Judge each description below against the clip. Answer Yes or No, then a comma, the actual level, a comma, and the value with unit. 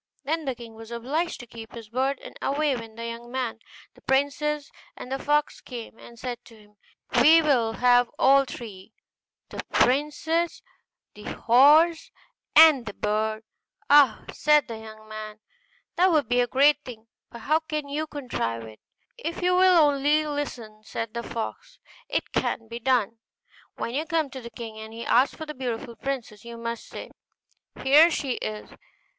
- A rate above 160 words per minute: Yes, average, 175 wpm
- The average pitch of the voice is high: Yes, very high, 250 Hz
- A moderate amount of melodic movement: Yes, average, 4.7 semitones